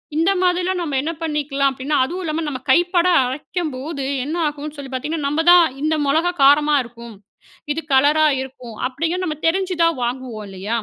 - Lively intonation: No, average, 3.8 semitones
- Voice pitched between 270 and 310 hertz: Yes, very high, 295 Hz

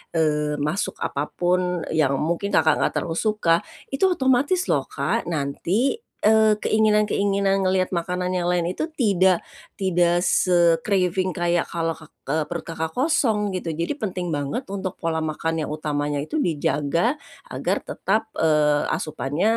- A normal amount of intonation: Yes, average, 4.1 semitones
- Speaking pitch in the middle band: Yes, medium, 175 Hz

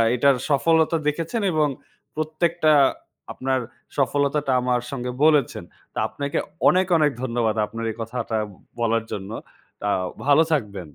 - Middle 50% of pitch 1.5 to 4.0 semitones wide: No, average, 5.1 semitones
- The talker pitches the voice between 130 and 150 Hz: Yes, medium, 140 Hz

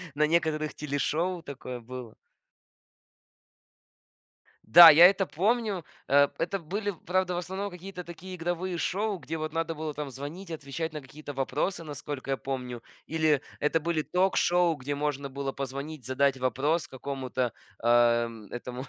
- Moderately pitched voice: Yes, medium, 155 Hz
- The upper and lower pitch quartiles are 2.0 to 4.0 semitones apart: No, average, 4.4 semitones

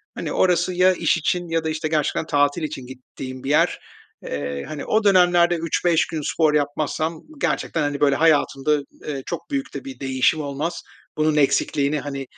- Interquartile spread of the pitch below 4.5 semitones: Yes, average, 2.9 semitones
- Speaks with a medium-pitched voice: Yes, medium, 155 Hz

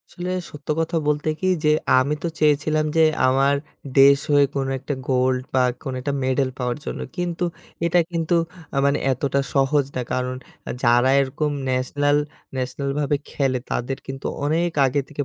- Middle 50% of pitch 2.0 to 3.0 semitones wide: Yes, narrow, 2.5 semitones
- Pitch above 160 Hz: No, medium, 140 Hz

